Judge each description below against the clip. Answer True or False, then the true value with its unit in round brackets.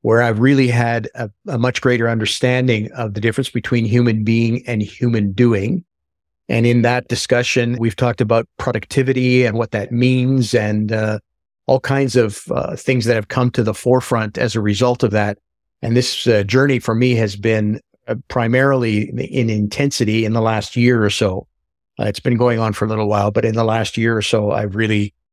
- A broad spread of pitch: False (2.7 semitones)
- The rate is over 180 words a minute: True (200 wpm)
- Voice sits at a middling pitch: False (115 Hz)